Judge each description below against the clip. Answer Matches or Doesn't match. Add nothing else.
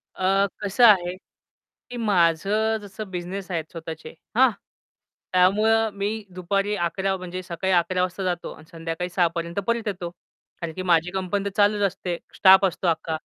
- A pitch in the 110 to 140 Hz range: Doesn't match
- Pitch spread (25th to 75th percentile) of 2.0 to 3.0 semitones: Matches